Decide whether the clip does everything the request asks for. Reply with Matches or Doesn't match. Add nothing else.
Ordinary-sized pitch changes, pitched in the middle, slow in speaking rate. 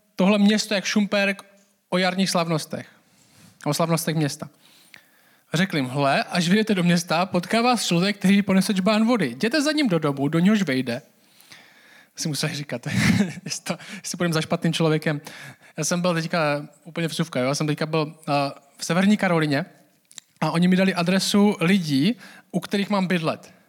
Doesn't match